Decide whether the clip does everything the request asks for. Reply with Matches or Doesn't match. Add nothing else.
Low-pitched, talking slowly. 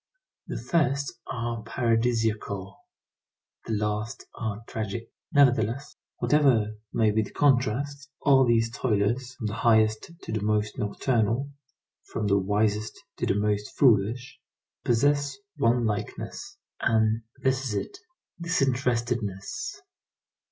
Matches